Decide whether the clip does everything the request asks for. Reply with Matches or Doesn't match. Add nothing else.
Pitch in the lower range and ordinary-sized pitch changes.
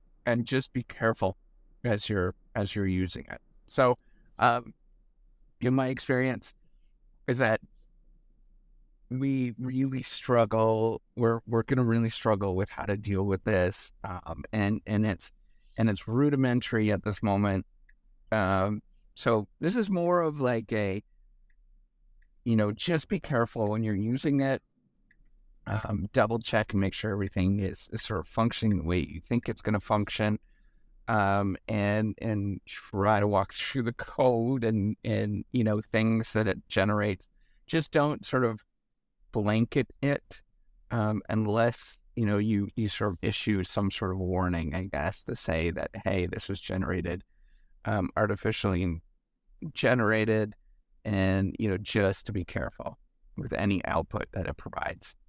Matches